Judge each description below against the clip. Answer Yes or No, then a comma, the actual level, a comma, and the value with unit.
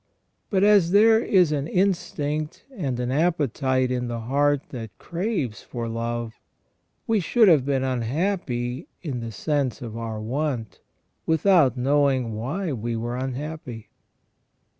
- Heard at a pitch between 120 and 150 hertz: Yes, low, 135 Hz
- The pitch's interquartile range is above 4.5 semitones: Yes, wide, 5.4 semitones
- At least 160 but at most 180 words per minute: No, slow, 135 wpm